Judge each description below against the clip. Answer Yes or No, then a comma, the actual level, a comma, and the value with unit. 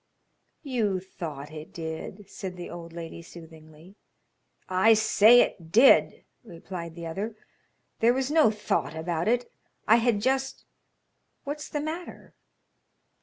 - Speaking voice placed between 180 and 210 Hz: Yes, high, 190 Hz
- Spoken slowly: Yes, slow, 125 wpm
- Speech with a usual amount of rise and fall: No, wide, 6.2 semitones